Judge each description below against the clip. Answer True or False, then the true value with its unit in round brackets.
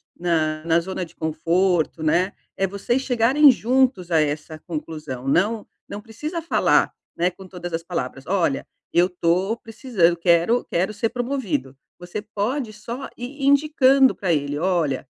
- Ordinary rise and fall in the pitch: False (6.1 semitones)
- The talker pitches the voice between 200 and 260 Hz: False (185 Hz)